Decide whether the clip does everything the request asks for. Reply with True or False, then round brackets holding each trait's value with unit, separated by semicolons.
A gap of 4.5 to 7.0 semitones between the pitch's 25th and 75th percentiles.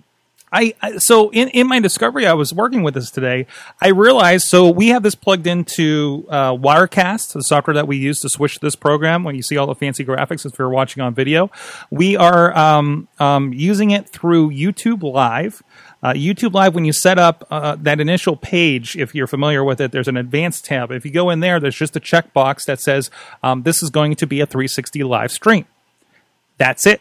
True (4.8 semitones)